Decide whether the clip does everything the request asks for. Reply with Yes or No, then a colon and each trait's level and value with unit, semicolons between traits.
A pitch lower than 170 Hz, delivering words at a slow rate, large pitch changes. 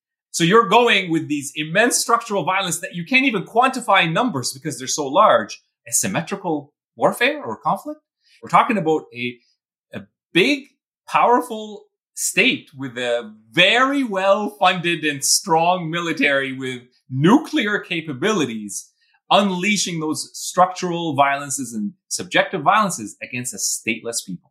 No: medium, 180 Hz; slow, 130 wpm; wide, 8.2 semitones